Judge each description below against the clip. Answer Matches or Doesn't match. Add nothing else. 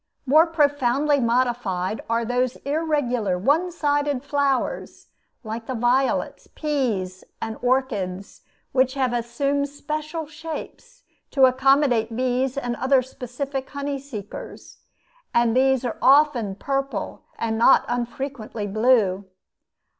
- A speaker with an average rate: Doesn't match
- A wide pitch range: Doesn't match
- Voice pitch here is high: Matches